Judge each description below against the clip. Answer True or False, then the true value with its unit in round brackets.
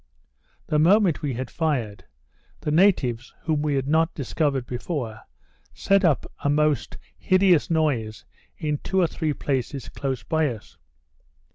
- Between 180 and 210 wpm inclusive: False (140 wpm)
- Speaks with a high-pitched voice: False (150 Hz)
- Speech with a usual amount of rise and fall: True (3.8 semitones)